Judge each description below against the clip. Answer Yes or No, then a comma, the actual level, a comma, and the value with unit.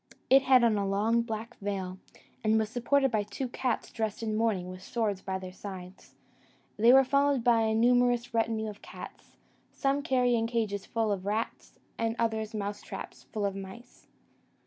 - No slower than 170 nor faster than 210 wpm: Yes, average, 180 wpm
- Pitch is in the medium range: No, high, 220 Hz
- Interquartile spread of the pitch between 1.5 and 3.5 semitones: Yes, average, 3.0 semitones